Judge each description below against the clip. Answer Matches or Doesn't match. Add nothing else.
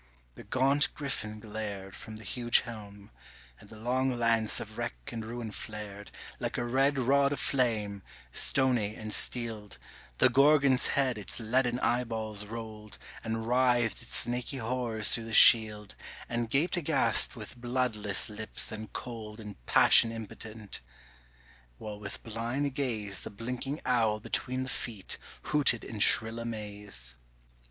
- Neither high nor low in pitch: Doesn't match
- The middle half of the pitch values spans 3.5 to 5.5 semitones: Doesn't match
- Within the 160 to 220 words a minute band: Doesn't match